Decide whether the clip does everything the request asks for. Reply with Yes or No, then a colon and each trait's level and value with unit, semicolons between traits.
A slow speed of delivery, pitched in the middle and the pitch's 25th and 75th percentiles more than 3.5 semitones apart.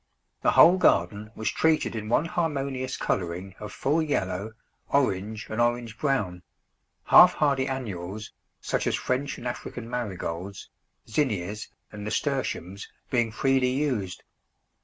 No: slow, 125 wpm; low, 115 Hz; average, 5.2 semitones